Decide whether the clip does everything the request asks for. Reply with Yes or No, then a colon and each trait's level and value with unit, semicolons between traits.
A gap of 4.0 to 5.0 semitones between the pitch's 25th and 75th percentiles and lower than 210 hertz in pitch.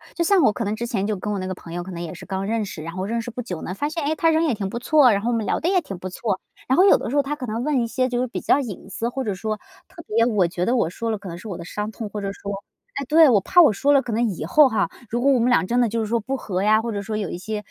No: average, 4.5 semitones; high, 225 Hz